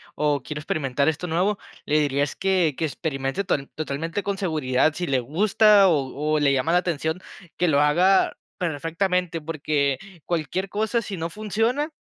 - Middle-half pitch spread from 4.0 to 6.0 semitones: Yes, average, 4.6 semitones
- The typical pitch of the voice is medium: Yes, medium, 160 Hz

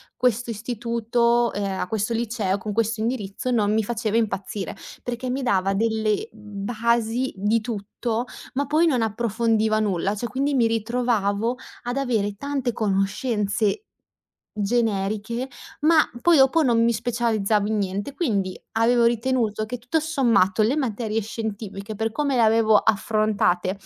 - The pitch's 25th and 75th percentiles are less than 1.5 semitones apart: No, average, 2.7 semitones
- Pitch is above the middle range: Yes, high, 225 Hz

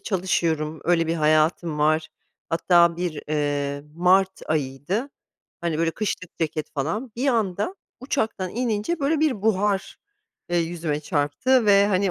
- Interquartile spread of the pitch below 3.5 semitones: No, average, 5.0 semitones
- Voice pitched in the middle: Yes, medium, 175 Hz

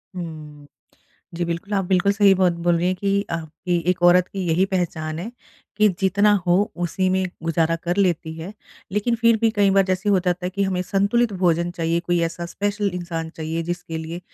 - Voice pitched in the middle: Yes, medium, 180 Hz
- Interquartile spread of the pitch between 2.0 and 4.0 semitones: Yes, average, 2.8 semitones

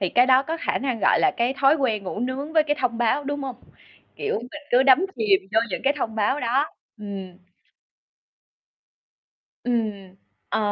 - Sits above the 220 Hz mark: Yes, high, 245 Hz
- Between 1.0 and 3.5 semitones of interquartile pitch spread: No, average, 4.3 semitones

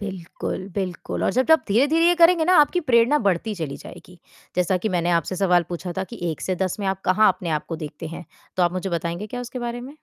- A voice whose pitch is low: No, high, 190 Hz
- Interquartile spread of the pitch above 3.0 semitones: Yes, wide, 5.6 semitones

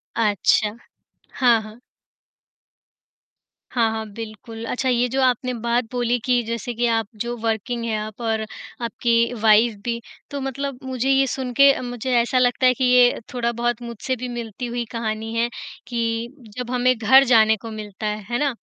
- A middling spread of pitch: No, narrow, 1.9 semitones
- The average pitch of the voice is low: No, high, 235 Hz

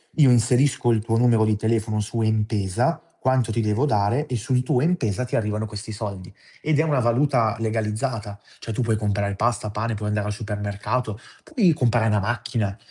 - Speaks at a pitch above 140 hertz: No, low, 110 Hz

